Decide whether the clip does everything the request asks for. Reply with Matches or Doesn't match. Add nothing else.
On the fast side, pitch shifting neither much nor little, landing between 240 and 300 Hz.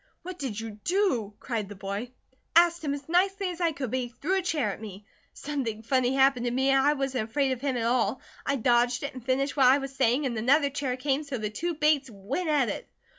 Matches